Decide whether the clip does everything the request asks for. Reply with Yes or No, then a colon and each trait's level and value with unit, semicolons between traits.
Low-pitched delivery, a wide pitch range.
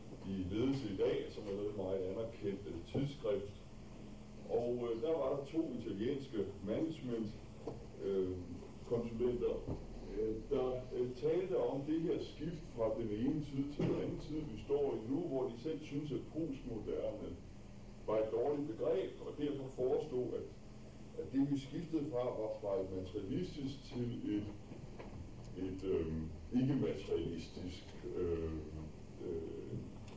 Yes: low, 115 Hz; wide, 5.8 semitones